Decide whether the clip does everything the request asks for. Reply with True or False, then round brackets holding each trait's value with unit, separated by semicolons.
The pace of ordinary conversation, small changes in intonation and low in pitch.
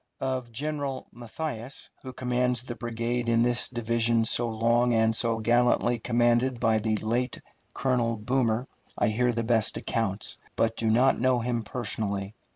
True (155 wpm; 1.7 semitones; 120 Hz)